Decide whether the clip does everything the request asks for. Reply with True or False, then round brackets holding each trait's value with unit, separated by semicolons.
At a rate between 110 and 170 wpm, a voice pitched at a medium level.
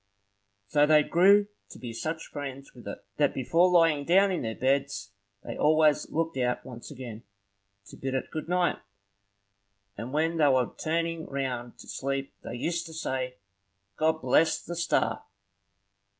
True (160 wpm; 145 Hz)